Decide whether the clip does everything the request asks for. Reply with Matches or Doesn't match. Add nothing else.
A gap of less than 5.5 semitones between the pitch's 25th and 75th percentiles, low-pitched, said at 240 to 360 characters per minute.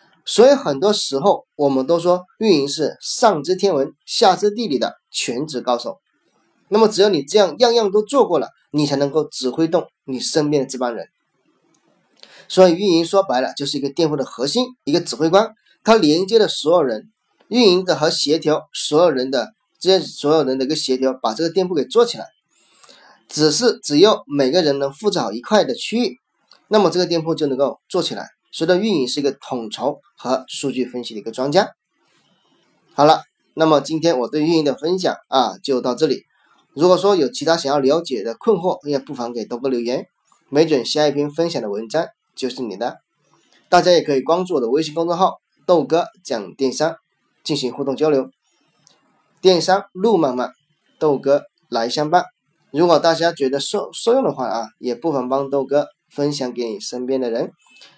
Doesn't match